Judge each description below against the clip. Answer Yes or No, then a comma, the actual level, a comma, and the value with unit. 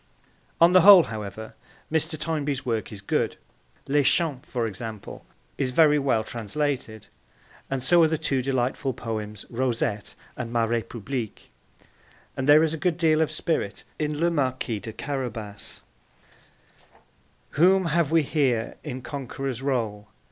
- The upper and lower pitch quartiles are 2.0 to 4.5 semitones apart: No, average, 5.3 semitones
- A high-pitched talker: No, low, 130 Hz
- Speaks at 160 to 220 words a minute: No, average, 140 wpm